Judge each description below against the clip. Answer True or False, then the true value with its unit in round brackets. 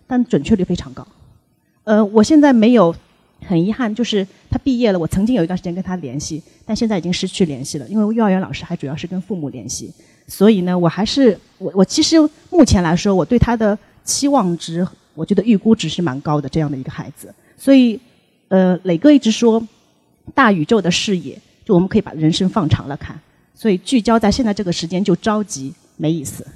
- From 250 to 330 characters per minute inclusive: True (320 characters per minute)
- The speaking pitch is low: False (190 Hz)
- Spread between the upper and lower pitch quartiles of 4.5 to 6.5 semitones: True (5.0 semitones)